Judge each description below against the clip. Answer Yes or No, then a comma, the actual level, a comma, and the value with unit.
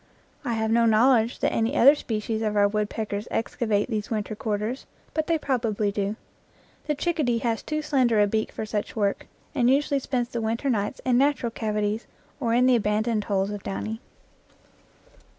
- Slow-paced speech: No, average, 175 wpm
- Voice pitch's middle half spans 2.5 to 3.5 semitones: Yes, average, 3.0 semitones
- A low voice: No, high, 225 Hz